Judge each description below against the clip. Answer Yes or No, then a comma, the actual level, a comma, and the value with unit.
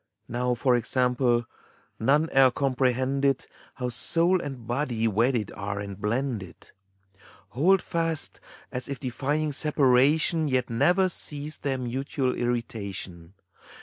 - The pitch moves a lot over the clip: No, average, 3.4 semitones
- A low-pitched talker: Yes, low, 130 Hz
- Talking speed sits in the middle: No, slow, 115 wpm